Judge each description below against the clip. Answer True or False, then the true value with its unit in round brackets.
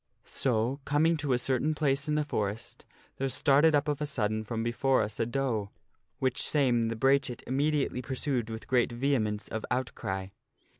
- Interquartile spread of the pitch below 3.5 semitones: False (3.8 semitones)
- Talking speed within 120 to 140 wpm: False (170 wpm)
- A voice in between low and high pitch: False (130 Hz)